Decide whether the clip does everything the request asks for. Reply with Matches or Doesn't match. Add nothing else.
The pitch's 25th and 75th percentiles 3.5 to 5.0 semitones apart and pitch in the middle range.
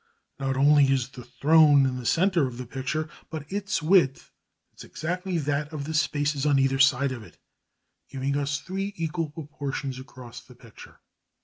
Doesn't match